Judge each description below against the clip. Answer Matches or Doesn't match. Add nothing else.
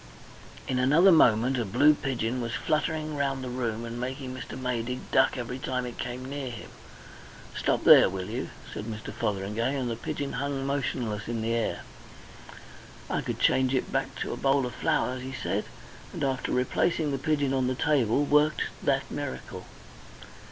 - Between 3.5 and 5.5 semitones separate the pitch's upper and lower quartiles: Doesn't match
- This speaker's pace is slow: Doesn't match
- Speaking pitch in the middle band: Doesn't match